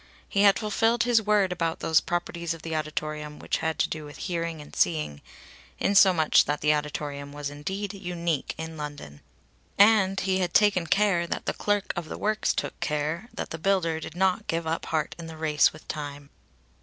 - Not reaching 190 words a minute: No, average, 200 wpm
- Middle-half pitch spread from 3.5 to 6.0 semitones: Yes, average, 4.1 semitones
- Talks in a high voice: No, medium, 165 Hz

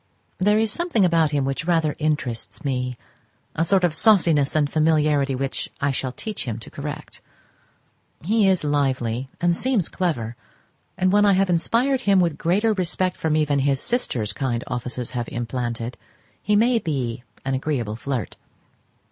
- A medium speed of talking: Yes, average, 165 wpm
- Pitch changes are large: Yes, wide, 6.1 semitones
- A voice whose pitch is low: No, medium, 150 Hz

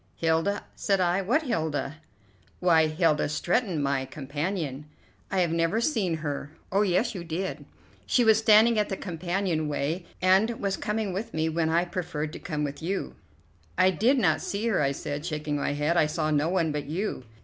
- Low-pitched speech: No, medium, 170 Hz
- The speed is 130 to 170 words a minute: No, average, 185 wpm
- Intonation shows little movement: No, average, 4.5 semitones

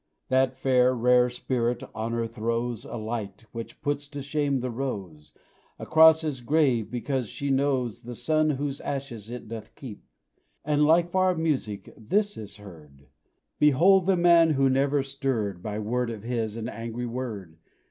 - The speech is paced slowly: No, average, 160 wpm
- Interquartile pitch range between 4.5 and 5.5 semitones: No, average, 4.1 semitones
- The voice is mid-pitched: No, low, 125 Hz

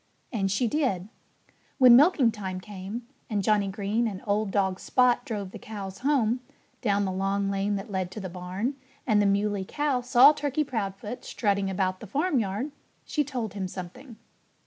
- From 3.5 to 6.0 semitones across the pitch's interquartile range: Yes, average, 4.2 semitones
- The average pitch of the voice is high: Yes, high, 205 Hz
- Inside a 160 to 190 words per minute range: Yes, average, 170 wpm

